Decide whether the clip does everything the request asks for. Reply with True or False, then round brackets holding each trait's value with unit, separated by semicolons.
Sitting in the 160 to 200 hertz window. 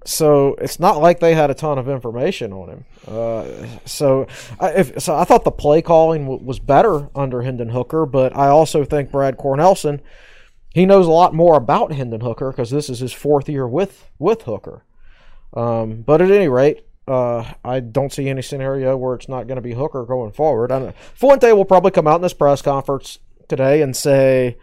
False (140 Hz)